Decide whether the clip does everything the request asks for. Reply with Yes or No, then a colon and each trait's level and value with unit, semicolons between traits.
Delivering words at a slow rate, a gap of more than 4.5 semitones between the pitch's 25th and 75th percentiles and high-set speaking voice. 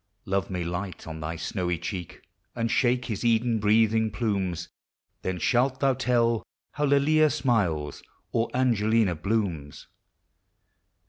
No: slow, 125 wpm; average, 5.1 semitones; low, 110 Hz